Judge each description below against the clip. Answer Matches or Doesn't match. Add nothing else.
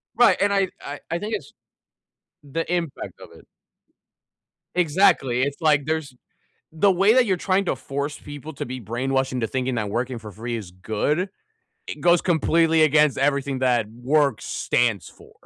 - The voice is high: Doesn't match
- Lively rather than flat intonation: Doesn't match